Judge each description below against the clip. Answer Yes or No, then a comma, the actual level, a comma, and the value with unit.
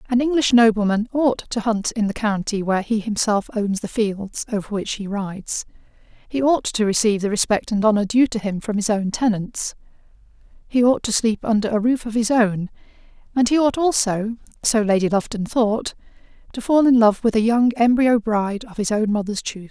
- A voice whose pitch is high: Yes, high, 220 Hz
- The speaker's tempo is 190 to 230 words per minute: Yes, average, 195 wpm